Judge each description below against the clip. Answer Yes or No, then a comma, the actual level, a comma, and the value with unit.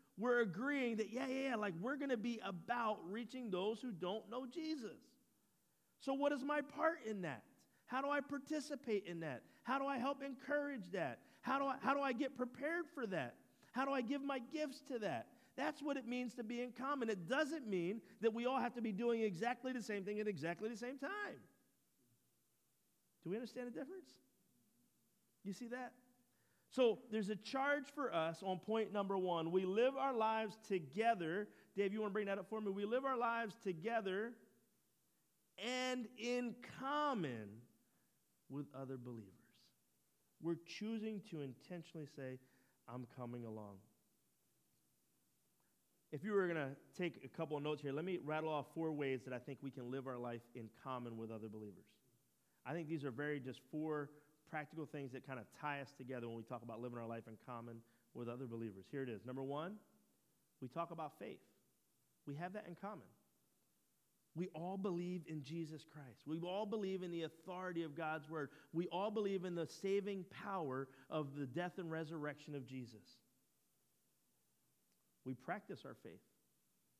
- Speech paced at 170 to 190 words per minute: Yes, average, 185 wpm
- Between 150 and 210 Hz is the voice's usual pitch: Yes, medium, 185 Hz